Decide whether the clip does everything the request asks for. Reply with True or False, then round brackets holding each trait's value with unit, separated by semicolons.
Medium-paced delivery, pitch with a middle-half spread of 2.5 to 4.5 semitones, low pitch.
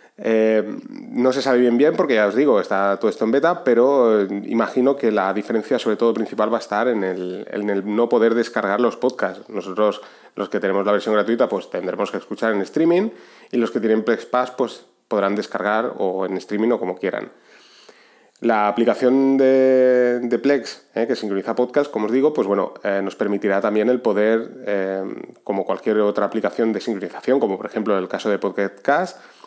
False (200 wpm; 3.5 semitones; 110 Hz)